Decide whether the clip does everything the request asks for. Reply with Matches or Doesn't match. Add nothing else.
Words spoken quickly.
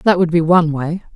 Matches